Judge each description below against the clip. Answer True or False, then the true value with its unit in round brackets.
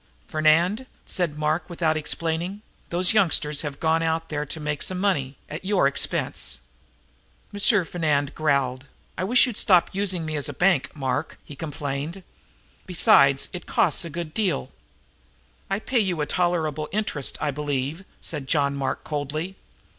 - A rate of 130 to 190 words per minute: True (155 wpm)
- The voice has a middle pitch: True (160 Hz)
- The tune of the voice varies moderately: True (3.9 semitones)